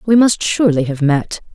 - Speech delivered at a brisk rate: No, average, 195 wpm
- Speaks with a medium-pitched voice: Yes, medium, 180 Hz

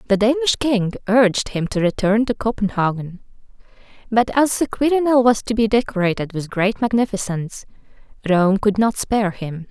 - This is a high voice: Yes, high, 215 Hz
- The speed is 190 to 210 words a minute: No, average, 155 wpm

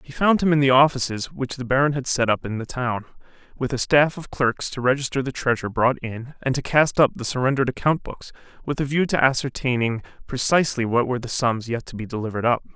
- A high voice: No, low, 130 Hz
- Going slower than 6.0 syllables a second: No, 6.1 syllables/s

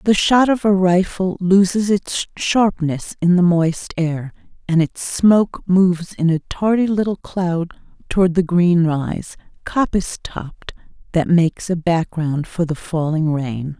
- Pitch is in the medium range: Yes, medium, 175 Hz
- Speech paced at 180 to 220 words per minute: No, average, 150 wpm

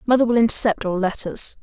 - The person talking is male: No, female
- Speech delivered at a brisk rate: No, average, 185 wpm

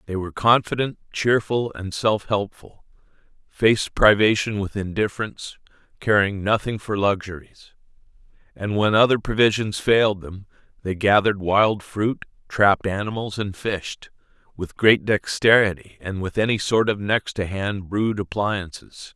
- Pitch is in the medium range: No, low, 105 Hz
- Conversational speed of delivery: No, slow, 130 wpm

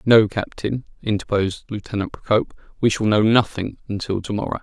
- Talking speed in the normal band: Yes, average, 155 wpm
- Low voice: Yes, low, 110 Hz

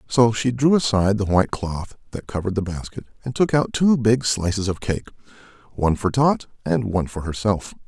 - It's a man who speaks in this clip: Yes, male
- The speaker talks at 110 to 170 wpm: No, average, 200 wpm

